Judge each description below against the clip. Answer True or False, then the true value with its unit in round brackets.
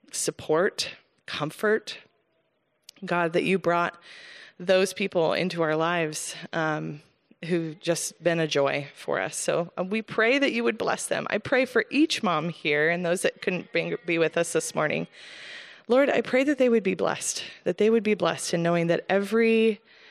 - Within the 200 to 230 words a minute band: False (175 wpm)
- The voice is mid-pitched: True (180 Hz)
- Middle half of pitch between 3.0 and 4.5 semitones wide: False (5.1 semitones)